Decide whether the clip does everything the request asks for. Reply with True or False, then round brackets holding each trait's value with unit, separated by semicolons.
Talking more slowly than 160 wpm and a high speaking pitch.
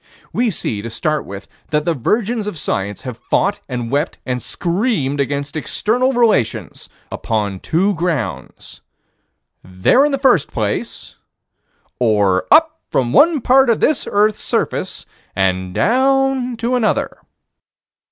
False (135 wpm; 170 Hz)